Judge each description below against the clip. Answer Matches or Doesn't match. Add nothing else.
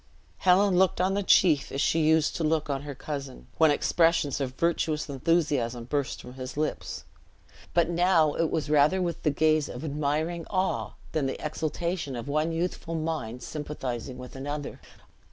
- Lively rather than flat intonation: Doesn't match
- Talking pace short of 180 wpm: Matches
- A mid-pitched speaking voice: Matches